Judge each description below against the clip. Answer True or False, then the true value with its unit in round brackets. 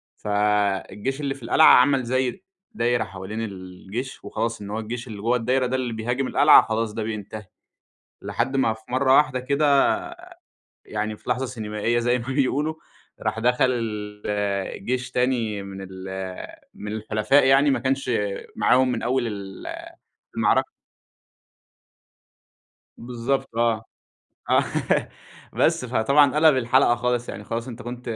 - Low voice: True (120 Hz)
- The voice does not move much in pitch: False (3.4 semitones)